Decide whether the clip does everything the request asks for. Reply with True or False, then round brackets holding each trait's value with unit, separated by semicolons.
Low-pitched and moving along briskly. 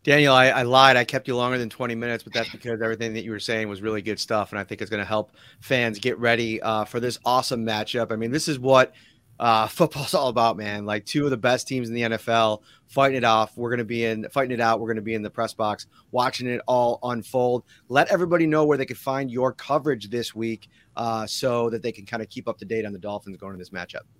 True (115 Hz; 270 wpm)